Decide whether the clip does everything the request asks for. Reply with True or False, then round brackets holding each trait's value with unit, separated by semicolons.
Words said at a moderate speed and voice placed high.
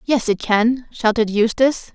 True (155 wpm; 230 Hz)